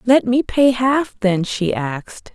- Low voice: No, high, 230 Hz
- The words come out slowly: No, average, 180 wpm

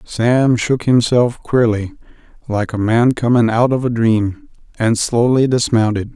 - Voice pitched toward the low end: Yes, low, 115 Hz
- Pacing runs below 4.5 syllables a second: Yes, 4.0 syllables/s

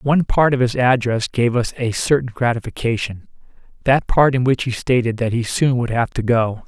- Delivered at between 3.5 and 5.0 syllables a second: No, 5.2 syllables/s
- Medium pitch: No, low, 120 Hz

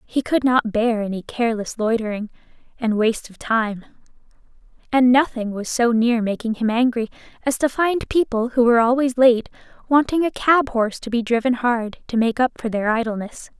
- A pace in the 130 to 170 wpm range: No, average, 180 wpm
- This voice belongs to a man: No, female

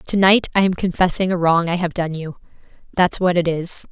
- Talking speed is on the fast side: Yes, fast, 230 wpm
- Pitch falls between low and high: Yes, medium, 175 Hz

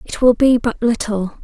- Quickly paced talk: Yes, fast, 210 wpm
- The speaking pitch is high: Yes, high, 230 Hz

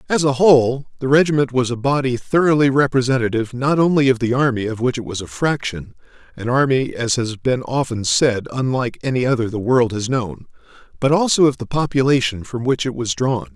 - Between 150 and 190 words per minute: No, average, 200 wpm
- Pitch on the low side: Yes, low, 130 Hz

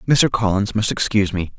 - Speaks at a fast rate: No, average, 190 wpm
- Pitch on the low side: Yes, low, 105 Hz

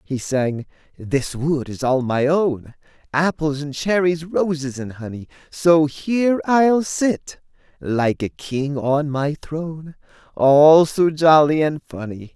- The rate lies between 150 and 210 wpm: No, average, 140 wpm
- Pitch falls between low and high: Yes, medium, 150 Hz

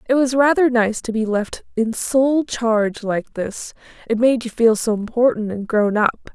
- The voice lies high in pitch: Yes, high, 230 Hz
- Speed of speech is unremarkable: Yes, average, 190 wpm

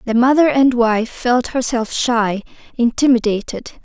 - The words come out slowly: Yes, slow, 125 wpm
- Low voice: No, high, 240 Hz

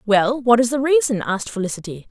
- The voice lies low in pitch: No, high, 230 Hz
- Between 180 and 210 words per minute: Yes, average, 200 wpm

